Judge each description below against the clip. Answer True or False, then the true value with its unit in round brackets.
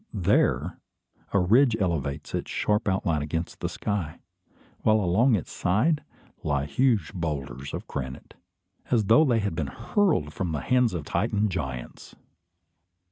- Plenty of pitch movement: True (6.8 semitones)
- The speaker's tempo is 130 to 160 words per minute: True (140 wpm)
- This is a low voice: True (90 Hz)